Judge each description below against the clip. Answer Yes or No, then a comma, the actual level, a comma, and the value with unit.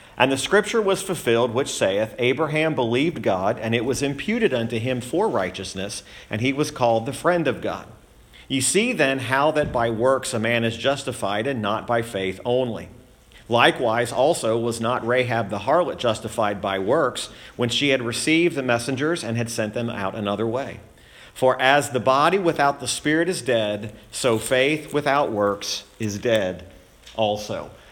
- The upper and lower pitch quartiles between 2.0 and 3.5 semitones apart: No, average, 4.0 semitones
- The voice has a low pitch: Yes, low, 120 Hz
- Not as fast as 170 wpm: No, average, 175 wpm